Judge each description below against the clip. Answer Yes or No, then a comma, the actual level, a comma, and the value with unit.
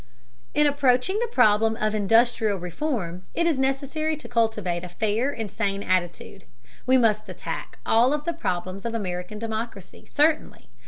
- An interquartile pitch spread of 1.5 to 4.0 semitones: No, wide, 5.5 semitones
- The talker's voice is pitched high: Yes, high, 225 Hz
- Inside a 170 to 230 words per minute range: No, average, 155 wpm